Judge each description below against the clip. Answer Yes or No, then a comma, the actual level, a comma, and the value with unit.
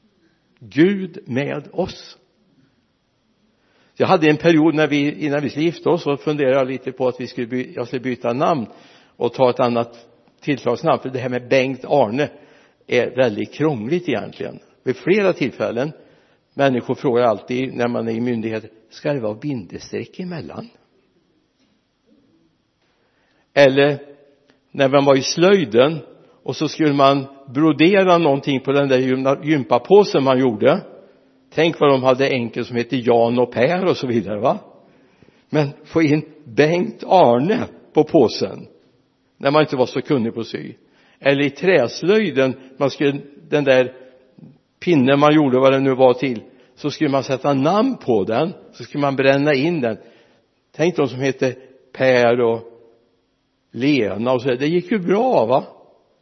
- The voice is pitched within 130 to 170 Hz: Yes, low, 135 Hz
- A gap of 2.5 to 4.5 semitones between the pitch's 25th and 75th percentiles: Yes, average, 2.8 semitones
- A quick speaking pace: No, average, 160 wpm